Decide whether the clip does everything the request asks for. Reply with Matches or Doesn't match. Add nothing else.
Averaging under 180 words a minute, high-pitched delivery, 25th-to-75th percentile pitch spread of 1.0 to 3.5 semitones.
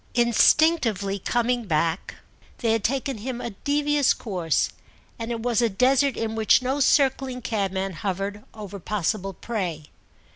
Doesn't match